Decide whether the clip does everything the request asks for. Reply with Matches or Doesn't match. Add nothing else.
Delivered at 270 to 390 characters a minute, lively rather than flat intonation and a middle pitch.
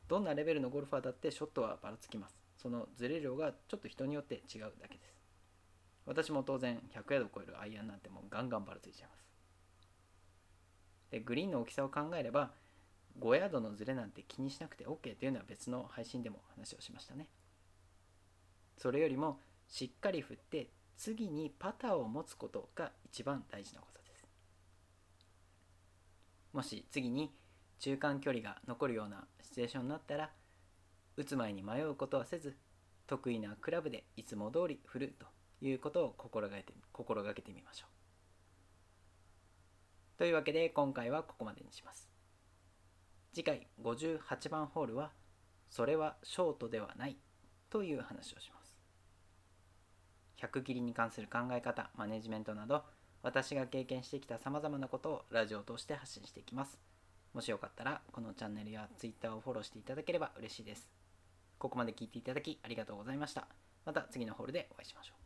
Doesn't match